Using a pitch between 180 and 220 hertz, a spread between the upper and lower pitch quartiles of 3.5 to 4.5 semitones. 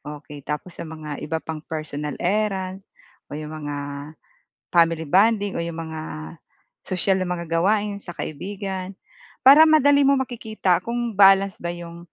Yes: medium, 185 Hz; average, 4.2 semitones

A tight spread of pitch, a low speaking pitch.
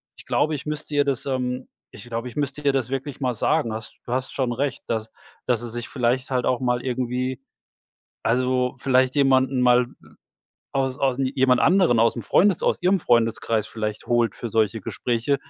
Yes: narrow, 2.3 semitones; low, 125 Hz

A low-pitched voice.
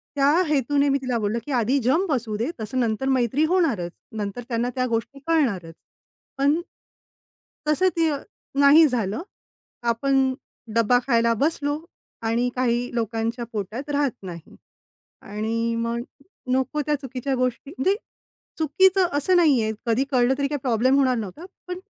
No: very high, 255 Hz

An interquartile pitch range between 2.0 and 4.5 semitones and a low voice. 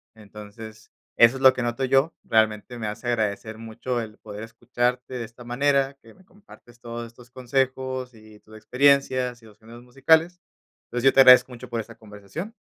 Yes: average, 2.8 semitones; low, 120 Hz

